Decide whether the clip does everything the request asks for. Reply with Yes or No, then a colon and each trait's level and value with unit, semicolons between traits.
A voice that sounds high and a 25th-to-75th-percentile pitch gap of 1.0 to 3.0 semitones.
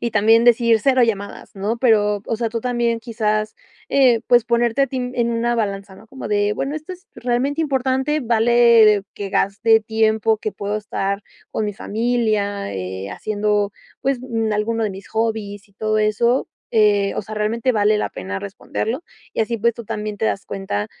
Yes: high, 220 Hz; narrow, 2.4 semitones